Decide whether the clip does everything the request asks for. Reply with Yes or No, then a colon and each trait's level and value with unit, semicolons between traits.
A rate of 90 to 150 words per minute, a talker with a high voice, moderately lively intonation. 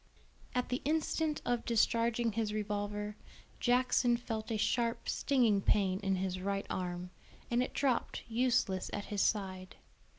Yes: average, 140 wpm; high, 220 Hz; average, 3.5 semitones